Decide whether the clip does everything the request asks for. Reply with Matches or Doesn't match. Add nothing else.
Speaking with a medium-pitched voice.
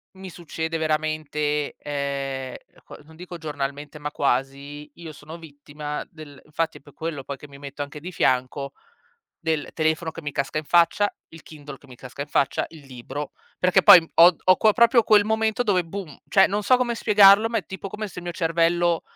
Matches